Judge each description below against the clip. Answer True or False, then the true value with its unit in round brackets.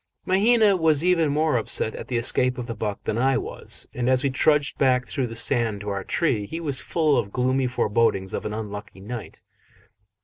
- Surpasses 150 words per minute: True (205 wpm)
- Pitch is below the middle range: True (125 Hz)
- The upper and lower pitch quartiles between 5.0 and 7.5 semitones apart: True (5.3 semitones)